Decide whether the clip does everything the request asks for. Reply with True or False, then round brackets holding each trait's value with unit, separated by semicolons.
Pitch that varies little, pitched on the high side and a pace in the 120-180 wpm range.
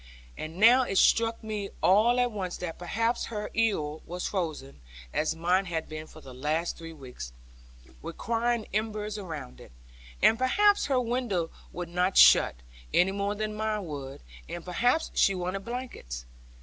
False (5.6 semitones; 195 Hz; 160 wpm)